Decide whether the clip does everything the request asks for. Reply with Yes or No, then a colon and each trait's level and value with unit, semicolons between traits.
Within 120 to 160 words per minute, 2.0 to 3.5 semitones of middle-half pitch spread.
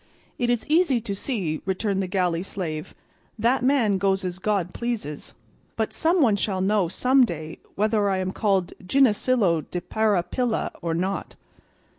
No: average, 155 wpm; average, 4.5 semitones